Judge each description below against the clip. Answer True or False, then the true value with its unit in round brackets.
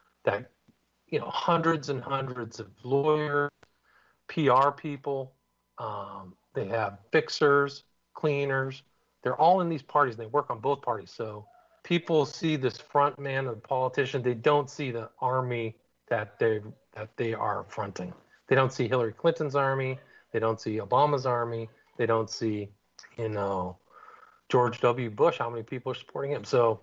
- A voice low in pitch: True (130 Hz)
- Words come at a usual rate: True (160 wpm)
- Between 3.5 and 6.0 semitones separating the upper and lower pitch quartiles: True (4.0 semitones)